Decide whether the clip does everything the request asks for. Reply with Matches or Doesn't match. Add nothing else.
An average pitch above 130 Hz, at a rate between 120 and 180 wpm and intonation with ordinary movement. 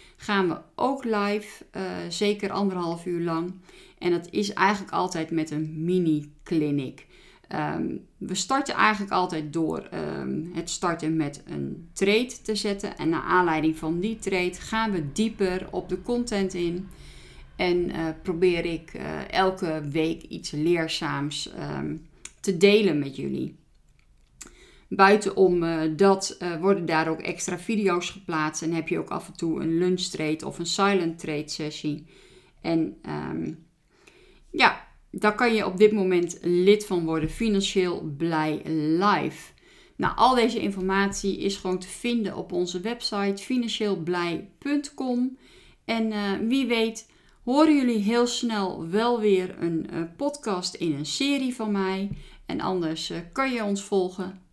Matches